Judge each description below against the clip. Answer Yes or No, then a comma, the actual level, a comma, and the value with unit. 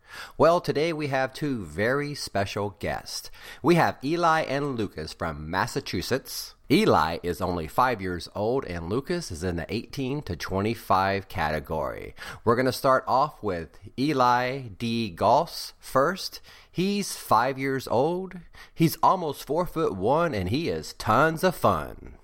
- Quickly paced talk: No, average, 150 wpm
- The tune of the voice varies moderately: No, wide, 7.3 semitones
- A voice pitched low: Yes, low, 115 Hz